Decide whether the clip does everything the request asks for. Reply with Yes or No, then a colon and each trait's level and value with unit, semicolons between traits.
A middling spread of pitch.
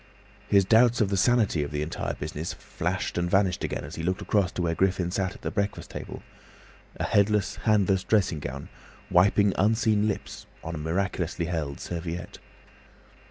Yes: average, 3.6 semitones